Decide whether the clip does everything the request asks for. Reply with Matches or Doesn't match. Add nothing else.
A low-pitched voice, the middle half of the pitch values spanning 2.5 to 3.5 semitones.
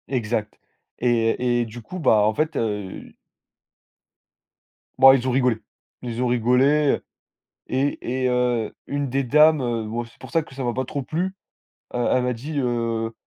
Matches